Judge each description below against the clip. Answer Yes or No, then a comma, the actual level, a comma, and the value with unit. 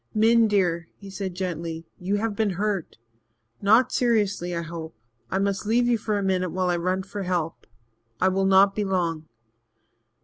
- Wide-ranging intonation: No, average, 2.8 semitones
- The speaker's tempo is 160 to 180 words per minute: Yes, average, 175 wpm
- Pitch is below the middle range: No, high, 190 Hz